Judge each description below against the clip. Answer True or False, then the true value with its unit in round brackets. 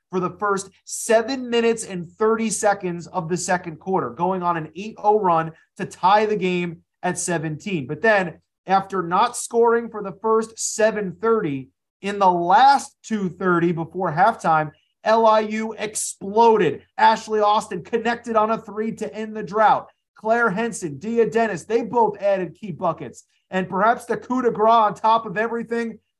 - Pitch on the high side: True (210 Hz)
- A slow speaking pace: False (160 wpm)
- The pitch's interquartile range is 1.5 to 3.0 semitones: False (3.7 semitones)